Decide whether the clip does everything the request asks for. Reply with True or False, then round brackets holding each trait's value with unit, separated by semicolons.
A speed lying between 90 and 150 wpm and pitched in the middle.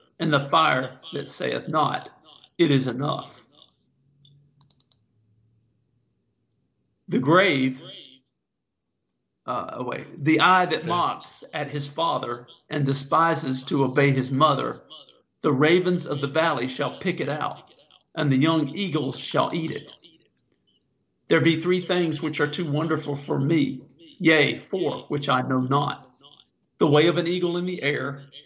True (140 wpm; 145 Hz)